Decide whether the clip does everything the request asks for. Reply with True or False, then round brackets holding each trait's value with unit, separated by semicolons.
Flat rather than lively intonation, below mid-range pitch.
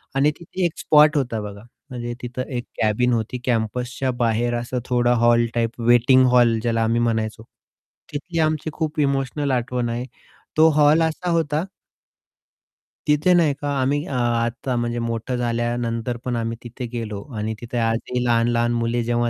False (3.0 semitones; 120 Hz)